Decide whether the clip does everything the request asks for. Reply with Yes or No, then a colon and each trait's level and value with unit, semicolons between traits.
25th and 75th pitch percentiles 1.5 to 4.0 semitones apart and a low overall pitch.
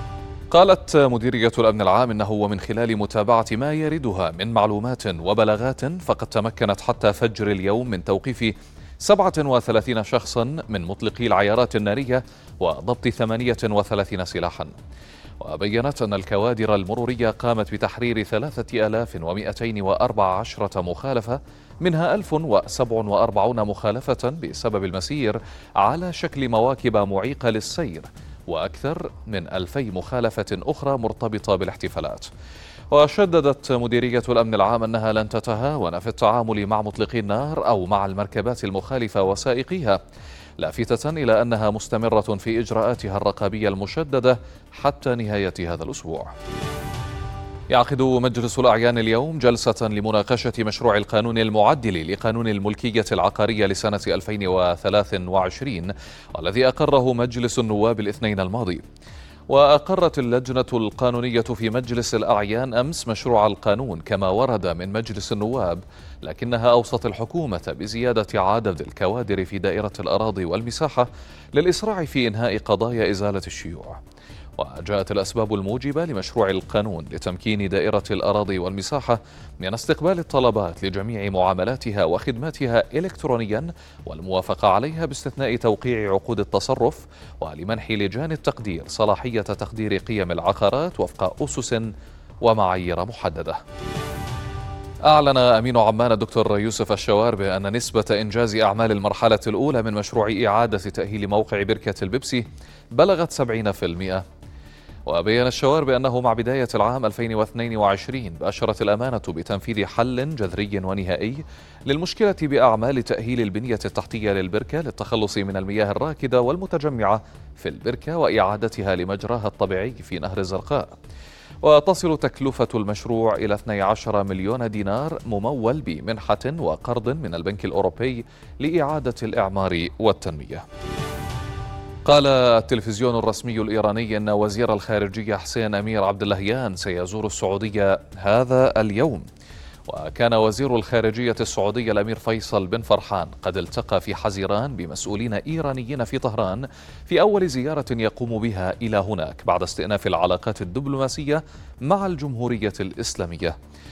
Yes: average, 3.6 semitones; low, 110 Hz